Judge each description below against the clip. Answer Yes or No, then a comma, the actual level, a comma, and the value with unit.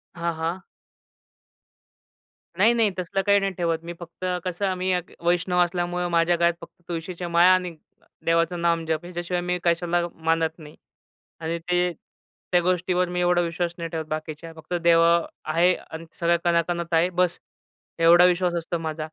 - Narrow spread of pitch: Yes, narrow, 1.2 semitones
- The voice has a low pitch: No, medium, 175 Hz